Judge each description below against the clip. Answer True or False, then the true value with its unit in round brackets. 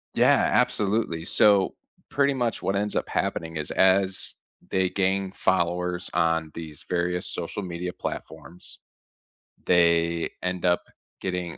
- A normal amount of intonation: False (2.3 semitones)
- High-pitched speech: False (90 Hz)